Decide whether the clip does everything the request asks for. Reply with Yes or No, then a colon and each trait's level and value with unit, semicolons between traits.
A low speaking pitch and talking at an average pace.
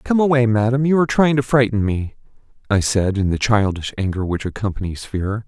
Yes: low, 115 Hz; average, 195 wpm